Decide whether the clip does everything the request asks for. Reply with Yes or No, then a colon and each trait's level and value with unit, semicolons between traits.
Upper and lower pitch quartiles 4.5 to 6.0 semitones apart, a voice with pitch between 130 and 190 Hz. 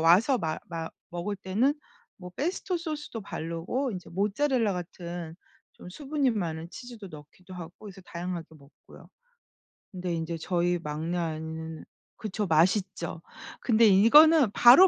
Yes: wide, 5.6 semitones; medium, 185 Hz